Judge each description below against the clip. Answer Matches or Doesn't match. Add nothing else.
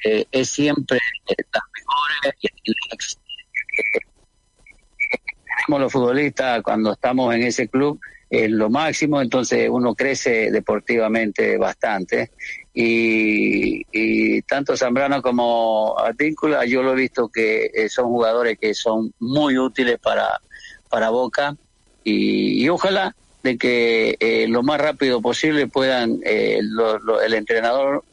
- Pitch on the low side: Matches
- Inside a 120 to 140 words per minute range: Matches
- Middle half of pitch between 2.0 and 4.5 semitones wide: Matches